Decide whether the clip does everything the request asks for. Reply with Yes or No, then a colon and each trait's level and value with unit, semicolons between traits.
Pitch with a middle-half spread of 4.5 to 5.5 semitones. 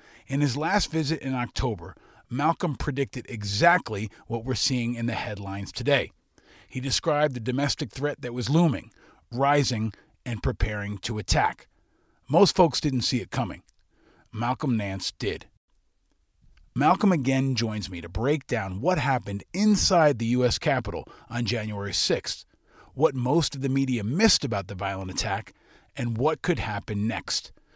Yes: average, 5.2 semitones